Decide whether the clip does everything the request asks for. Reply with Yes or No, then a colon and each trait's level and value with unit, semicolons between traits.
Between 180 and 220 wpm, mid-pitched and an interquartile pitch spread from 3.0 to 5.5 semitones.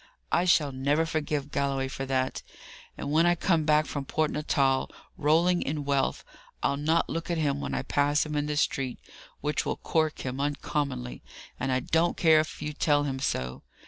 No: average, 190 wpm; medium, 145 Hz; narrow, 2.4 semitones